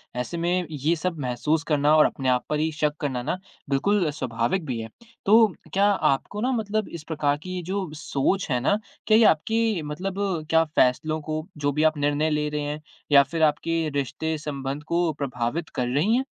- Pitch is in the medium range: Yes, medium, 155 Hz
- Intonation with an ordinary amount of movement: Yes, average, 3.7 semitones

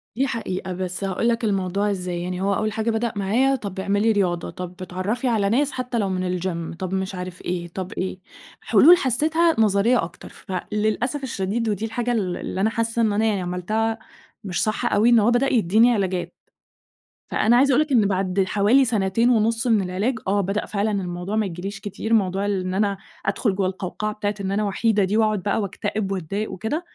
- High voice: Yes, high, 205 Hz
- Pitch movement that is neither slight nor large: Yes, average, 3.2 semitones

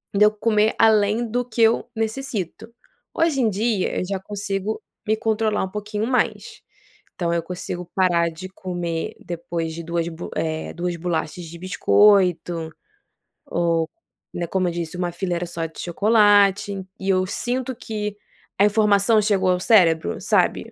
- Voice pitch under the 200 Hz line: Yes, high, 190 Hz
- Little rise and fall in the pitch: No, average, 3.8 semitones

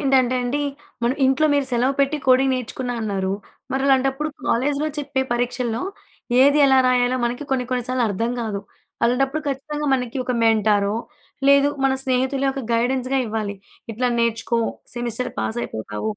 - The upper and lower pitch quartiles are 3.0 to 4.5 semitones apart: No, narrow, 2.6 semitones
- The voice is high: Yes, very high, 250 Hz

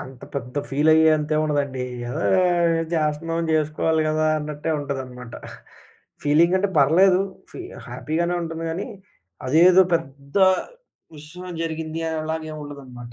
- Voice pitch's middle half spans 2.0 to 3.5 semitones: Yes, narrow, 2.6 semitones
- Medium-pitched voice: Yes, medium, 155 Hz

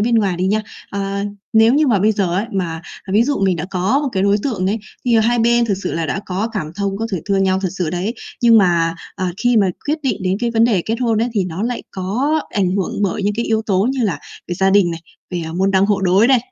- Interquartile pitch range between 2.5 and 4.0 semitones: Yes, average, 3.5 semitones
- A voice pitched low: No, high, 200 Hz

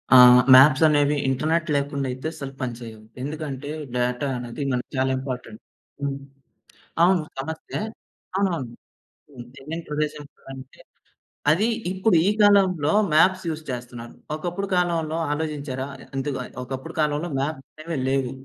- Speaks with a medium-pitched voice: Yes, medium, 145 Hz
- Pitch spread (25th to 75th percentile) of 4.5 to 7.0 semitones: No, average, 3.4 semitones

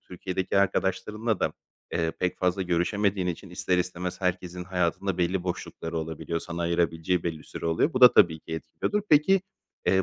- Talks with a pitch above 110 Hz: No, very low, 90 Hz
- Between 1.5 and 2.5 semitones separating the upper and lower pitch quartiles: Yes, narrow, 2.2 semitones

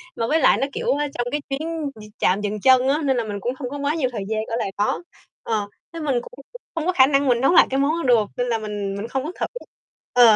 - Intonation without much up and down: No, average, 4.5 semitones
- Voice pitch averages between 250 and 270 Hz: Yes, very high, 255 Hz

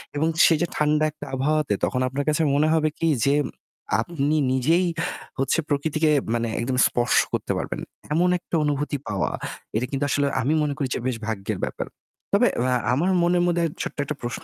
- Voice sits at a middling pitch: Yes, medium, 145 Hz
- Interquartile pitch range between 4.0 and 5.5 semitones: No, average, 3.4 semitones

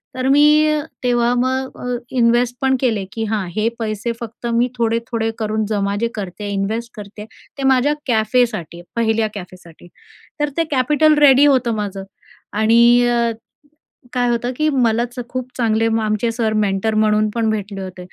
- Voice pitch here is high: Yes, high, 230 Hz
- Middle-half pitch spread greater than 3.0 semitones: No, average, 2.7 semitones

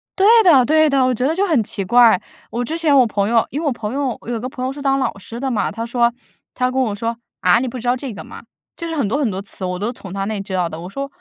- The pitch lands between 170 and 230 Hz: No, high, 245 Hz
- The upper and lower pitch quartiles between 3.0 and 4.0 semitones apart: No, average, 4.6 semitones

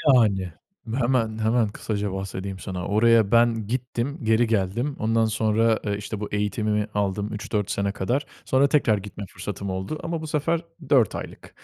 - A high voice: No, low, 110 Hz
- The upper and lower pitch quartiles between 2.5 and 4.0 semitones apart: Yes, average, 2.8 semitones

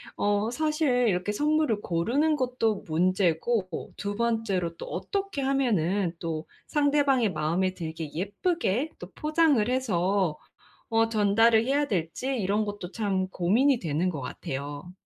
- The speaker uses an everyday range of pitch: No, wide, 6.5 semitones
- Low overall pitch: No, high, 205 Hz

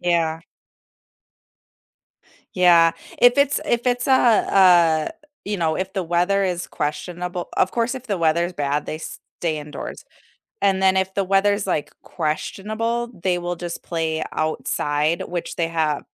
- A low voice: No, medium, 175 Hz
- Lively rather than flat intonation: No, average, 3.4 semitones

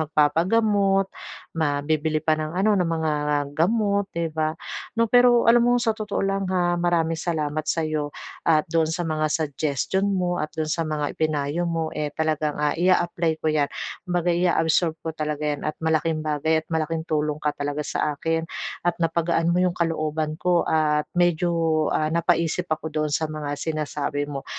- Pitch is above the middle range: No, medium, 160 Hz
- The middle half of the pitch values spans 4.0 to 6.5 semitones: No, narrow, 2.4 semitones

